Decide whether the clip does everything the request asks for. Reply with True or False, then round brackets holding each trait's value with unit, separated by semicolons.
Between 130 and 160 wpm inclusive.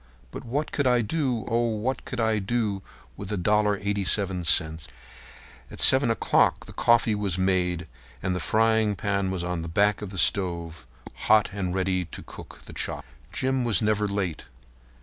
False (180 wpm)